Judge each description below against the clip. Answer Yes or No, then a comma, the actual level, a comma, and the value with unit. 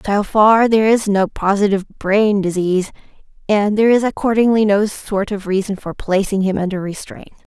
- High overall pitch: Yes, high, 205 Hz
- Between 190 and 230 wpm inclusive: No, average, 165 wpm